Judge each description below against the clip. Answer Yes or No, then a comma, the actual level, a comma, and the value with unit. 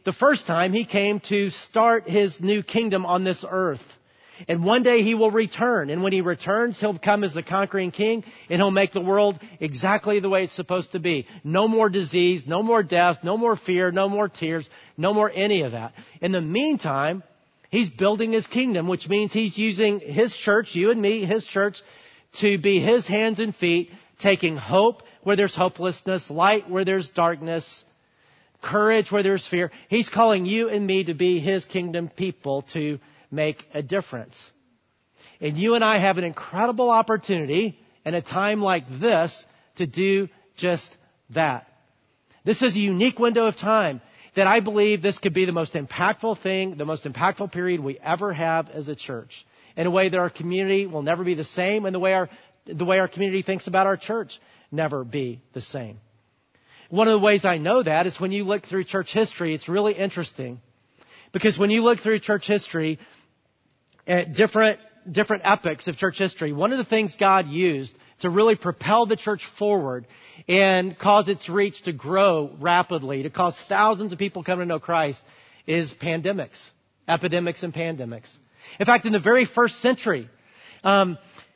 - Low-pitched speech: No, high, 190 Hz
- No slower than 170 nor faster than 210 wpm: Yes, average, 185 wpm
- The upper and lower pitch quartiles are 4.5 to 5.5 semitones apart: No, average, 3.9 semitones